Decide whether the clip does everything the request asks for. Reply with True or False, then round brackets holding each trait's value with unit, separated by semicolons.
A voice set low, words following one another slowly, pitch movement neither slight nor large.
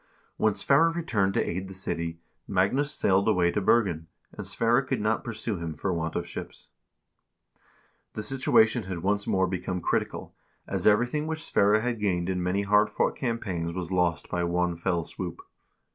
False (95 Hz; 175 wpm; 4.2 semitones)